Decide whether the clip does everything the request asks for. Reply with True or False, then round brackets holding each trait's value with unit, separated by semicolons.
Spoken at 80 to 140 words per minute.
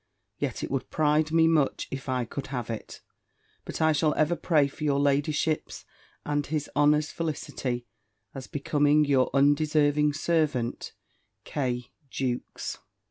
True (135 wpm)